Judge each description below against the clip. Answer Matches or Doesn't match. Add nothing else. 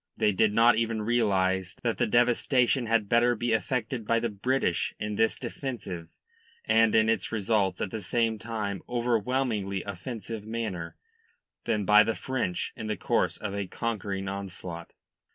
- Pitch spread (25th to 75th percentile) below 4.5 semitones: Matches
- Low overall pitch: Matches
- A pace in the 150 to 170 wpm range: Matches